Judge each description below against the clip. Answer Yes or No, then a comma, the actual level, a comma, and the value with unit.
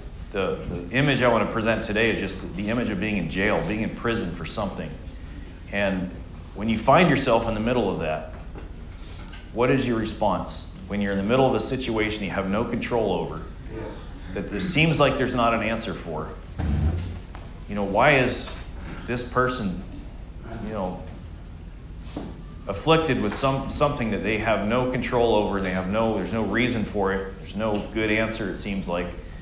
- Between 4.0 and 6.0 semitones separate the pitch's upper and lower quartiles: Yes, average, 4.8 semitones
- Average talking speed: Yes, average, 185 wpm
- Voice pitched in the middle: No, low, 100 Hz